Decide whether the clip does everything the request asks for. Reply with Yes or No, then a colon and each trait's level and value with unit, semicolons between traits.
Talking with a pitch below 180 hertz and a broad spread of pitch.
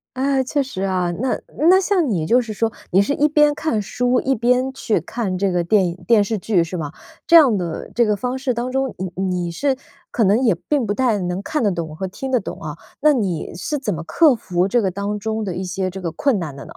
No: high, 215 Hz; wide, 6.0 semitones